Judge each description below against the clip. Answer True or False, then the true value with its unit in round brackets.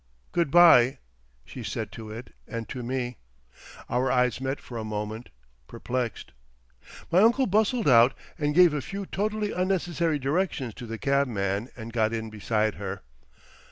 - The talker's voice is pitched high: False (125 Hz)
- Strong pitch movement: True (7.1 semitones)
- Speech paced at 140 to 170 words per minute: True (150 wpm)